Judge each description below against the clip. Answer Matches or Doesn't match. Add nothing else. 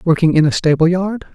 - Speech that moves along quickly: Matches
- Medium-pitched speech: Matches